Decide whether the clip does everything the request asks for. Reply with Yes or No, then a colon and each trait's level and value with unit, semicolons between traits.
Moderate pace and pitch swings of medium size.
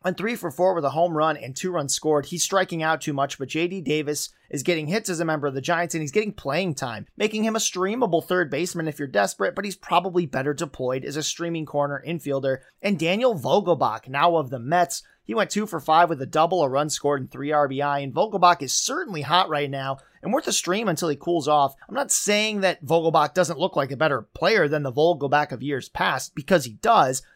No: fast, 240 wpm; average, 4.0 semitones